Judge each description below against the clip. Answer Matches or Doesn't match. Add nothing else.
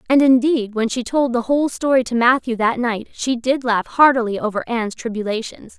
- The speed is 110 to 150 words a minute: Doesn't match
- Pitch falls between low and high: Doesn't match